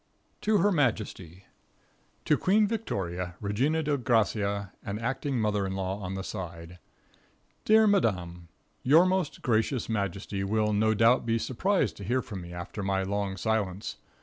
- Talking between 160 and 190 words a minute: No, average, 150 wpm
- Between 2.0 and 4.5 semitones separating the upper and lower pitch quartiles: No, wide, 5.5 semitones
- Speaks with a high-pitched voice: No, low, 105 Hz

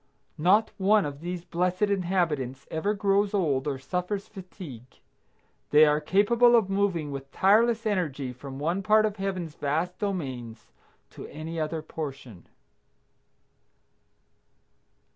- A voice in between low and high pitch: Yes, medium, 175 Hz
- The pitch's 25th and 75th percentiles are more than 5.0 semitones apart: Yes, wide, 5.4 semitones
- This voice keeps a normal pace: No, slow, 125 wpm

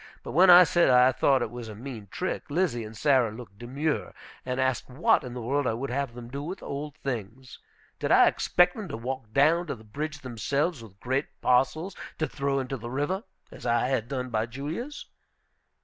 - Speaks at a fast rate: Yes, fast, 210 wpm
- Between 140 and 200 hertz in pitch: No, low, 130 Hz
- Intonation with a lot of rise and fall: No, average, 3.8 semitones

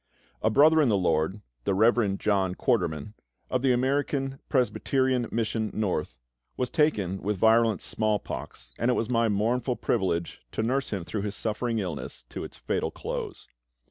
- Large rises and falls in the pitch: No, average, 4.1 semitones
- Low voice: Yes, low, 110 Hz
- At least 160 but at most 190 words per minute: Yes, average, 165 wpm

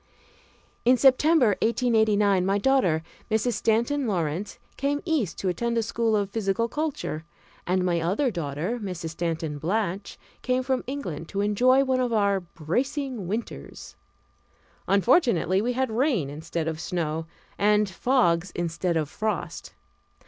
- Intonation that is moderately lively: No, wide, 6.3 semitones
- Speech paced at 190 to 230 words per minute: No, slow, 135 wpm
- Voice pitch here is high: Yes, high, 205 Hz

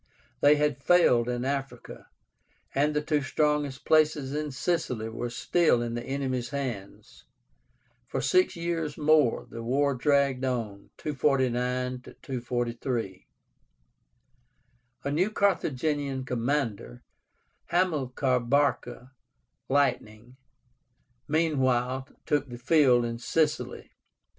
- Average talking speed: No, slow, 100 wpm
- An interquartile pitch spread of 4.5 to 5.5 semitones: No, average, 3.4 semitones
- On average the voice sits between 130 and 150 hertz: Yes, low, 135 Hz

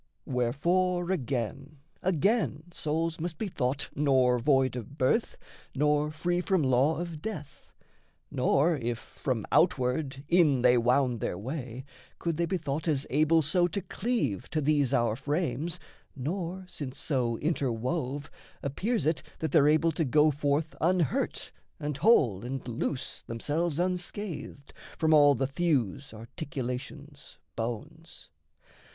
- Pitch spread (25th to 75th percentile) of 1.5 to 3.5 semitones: No, average, 4.4 semitones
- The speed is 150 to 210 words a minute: No, slow, 135 wpm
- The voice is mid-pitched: Yes, medium, 145 Hz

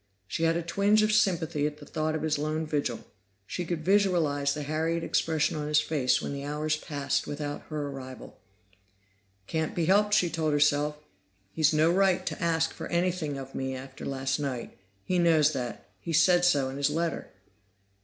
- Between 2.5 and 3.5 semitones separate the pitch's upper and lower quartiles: Yes, average, 2.8 semitones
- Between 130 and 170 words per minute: No, average, 185 wpm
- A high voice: No, medium, 155 Hz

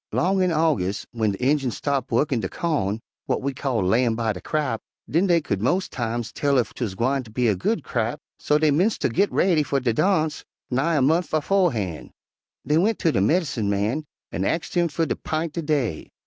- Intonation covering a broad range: Yes, wide, 6.2 semitones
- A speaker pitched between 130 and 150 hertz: Yes, medium, 140 Hz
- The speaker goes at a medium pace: No, fast, 210 wpm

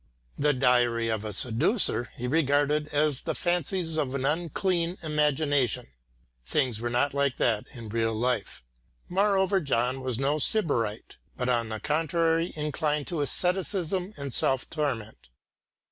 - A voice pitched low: No, medium, 145 Hz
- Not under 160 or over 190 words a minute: No, average, 140 wpm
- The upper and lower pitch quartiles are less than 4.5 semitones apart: No, average, 5.1 semitones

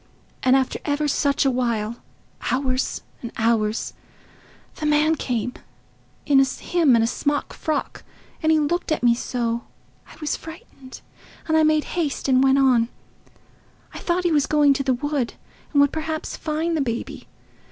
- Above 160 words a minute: No, average, 150 wpm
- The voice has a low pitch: No, very high, 280 Hz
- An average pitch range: Yes, average, 3.7 semitones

